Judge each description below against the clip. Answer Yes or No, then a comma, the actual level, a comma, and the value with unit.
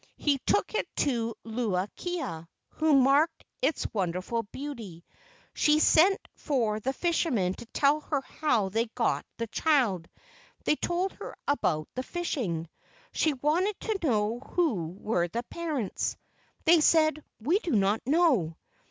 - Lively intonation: Yes, wide, 6.9 semitones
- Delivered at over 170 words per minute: No, average, 140 wpm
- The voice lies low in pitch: No, very high, 260 Hz